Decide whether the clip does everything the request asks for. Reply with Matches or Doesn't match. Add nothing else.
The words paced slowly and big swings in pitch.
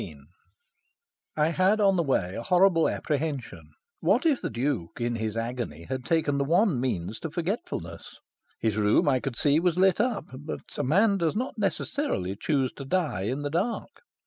Doesn't match